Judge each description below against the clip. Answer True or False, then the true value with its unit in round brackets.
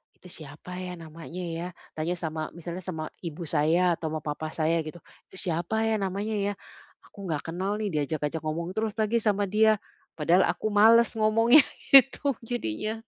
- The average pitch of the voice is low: False (180 Hz)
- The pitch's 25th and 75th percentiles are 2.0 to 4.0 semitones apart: False (5.2 semitones)